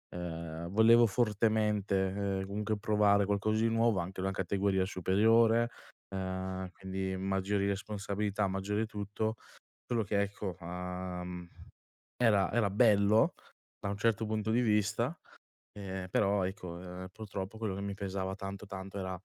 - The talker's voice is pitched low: Yes, low, 100 Hz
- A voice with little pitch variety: Yes, narrow, 2.1 semitones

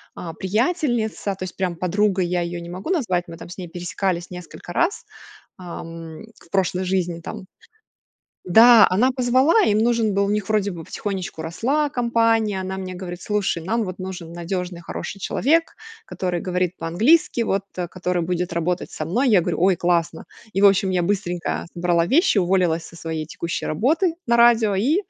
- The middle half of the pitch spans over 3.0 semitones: Yes, average, 4.0 semitones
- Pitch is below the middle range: No, medium, 185 Hz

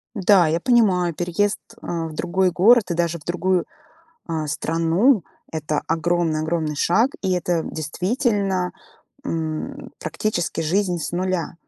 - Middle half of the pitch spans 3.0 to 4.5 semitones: No, narrow, 2.6 semitones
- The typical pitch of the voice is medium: Yes, medium, 175 Hz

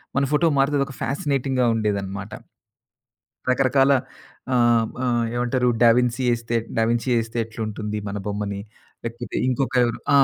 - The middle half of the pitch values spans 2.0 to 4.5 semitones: Yes, average, 2.9 semitones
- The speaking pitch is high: No, low, 120 Hz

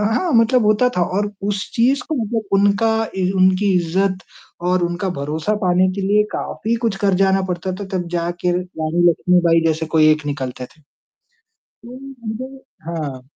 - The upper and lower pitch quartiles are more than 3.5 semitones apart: Yes, average, 4.0 semitones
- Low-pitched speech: No, medium, 185 Hz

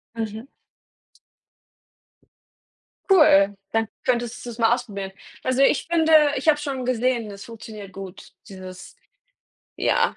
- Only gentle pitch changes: No, average, 4.4 semitones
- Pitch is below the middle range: No, high, 230 Hz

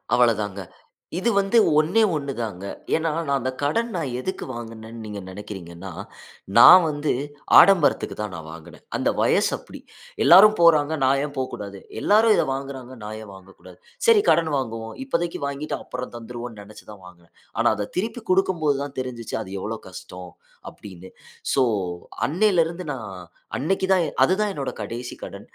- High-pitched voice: No, low, 130 Hz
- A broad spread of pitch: Yes, wide, 8.1 semitones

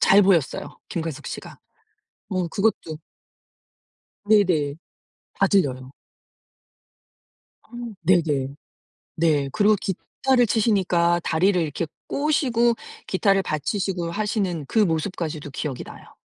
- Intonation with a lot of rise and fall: No, average, 4.7 semitones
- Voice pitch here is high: No, medium, 180 Hz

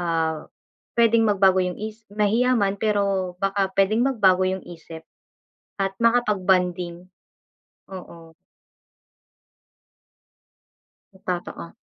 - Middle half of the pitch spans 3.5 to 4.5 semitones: No, average, 2.9 semitones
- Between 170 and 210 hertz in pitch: Yes, high, 190 Hz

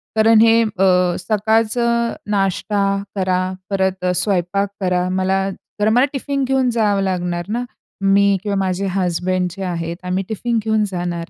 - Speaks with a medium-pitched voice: No, high, 195 Hz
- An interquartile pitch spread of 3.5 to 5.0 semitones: No, average, 3.1 semitones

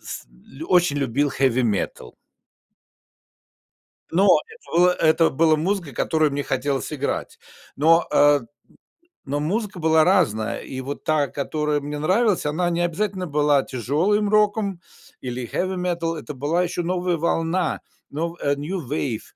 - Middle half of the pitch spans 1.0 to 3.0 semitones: No, average, 3.9 semitones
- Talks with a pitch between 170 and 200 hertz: No, medium, 160 Hz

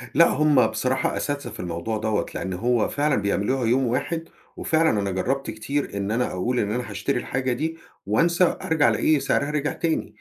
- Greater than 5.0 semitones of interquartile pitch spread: Yes, wide, 5.4 semitones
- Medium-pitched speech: No, low, 130 Hz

